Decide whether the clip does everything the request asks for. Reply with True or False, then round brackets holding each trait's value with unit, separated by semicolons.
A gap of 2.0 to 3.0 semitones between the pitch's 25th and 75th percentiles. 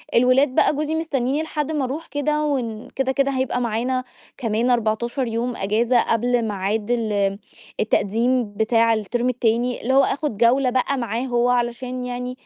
True (2.4 semitones)